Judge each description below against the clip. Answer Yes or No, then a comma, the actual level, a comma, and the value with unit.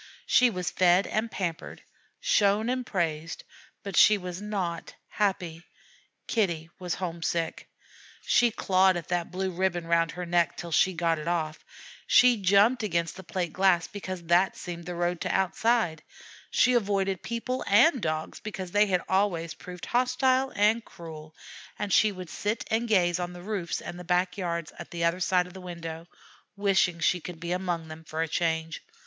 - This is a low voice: No, medium, 180 Hz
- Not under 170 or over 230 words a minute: Yes, average, 175 wpm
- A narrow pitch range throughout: No, average, 3.2 semitones